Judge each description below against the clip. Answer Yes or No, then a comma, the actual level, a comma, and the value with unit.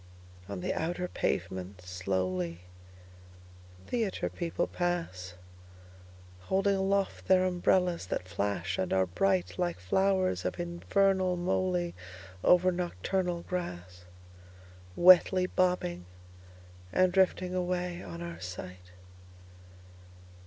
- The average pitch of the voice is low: Yes, very low, 95 Hz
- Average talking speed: No, slow, 80 wpm